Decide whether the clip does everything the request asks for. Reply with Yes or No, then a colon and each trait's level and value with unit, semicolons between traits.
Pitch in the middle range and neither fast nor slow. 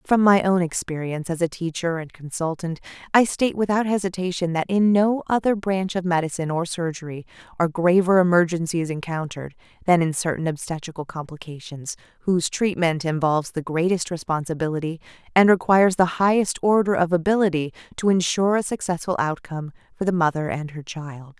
Yes: medium, 175 Hz; average, 155 wpm